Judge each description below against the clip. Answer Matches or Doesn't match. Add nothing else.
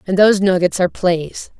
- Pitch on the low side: Doesn't match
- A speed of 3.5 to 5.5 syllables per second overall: Doesn't match